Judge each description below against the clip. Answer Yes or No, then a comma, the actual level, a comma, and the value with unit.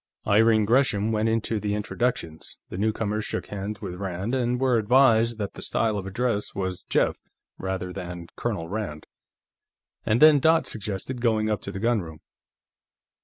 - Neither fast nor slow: Yes, average, 160 wpm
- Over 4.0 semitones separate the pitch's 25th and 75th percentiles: No, average, 3.1 semitones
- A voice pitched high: No, low, 105 Hz